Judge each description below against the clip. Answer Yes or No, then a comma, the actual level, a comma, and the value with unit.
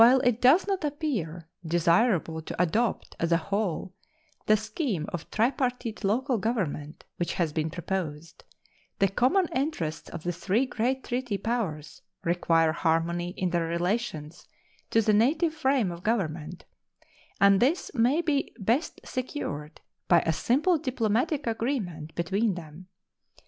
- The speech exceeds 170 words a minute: No, average, 140 wpm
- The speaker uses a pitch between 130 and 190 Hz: No, high, 200 Hz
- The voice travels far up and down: Yes, wide, 6.8 semitones